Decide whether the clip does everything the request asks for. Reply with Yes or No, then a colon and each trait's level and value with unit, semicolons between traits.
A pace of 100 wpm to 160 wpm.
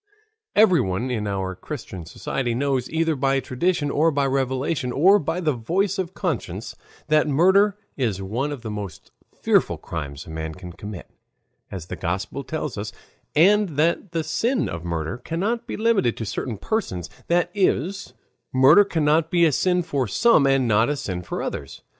No: average, 170 wpm